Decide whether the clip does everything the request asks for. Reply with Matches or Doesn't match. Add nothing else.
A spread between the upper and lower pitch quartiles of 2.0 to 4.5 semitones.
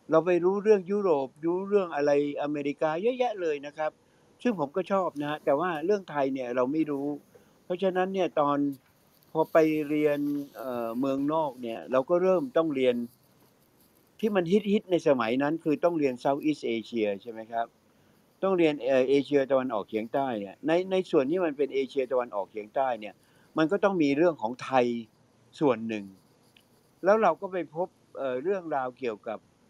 Doesn't match